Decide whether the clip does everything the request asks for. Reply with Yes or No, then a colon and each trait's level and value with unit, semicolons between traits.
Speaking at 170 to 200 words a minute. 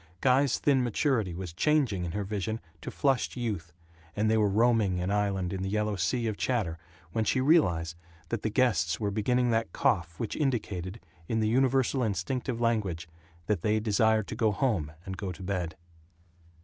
Yes: average, 180 wpm